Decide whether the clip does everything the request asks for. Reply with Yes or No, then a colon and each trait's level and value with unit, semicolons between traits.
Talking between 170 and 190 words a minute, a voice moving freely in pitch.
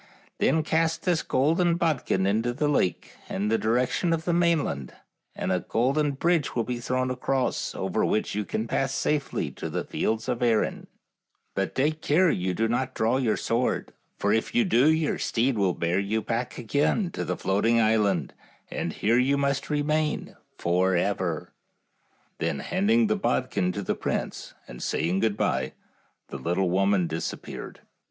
Yes: average, 175 wpm; wide, 7.1 semitones